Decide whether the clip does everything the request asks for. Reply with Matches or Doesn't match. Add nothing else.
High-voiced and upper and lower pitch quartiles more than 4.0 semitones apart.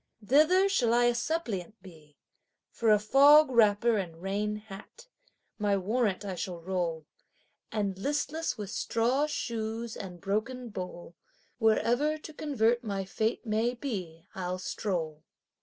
Matches